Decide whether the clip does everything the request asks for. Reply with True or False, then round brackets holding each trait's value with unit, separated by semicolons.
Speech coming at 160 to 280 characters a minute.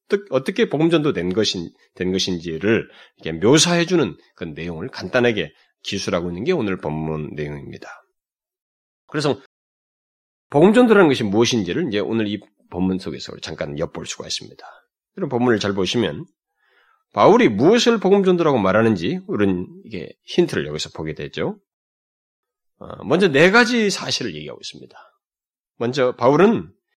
False (320 characters per minute)